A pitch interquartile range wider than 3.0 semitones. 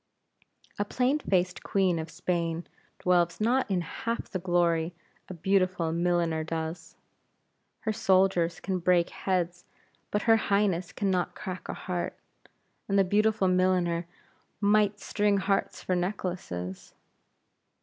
No: narrow, 2.6 semitones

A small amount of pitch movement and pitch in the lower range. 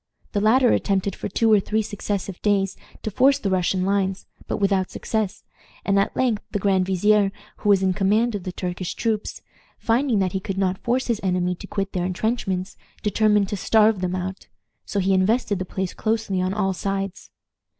No: narrow, 2.3 semitones; high, 195 Hz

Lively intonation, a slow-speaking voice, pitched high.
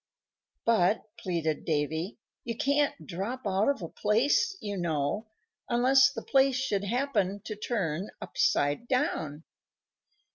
Yes: wide, 6.9 semitones; slow, 120 wpm; high, 210 Hz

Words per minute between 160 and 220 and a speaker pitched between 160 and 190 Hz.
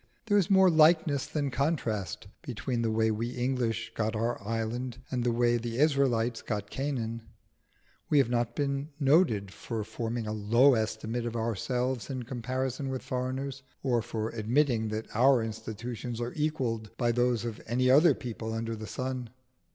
No: average, 165 wpm; low, 120 Hz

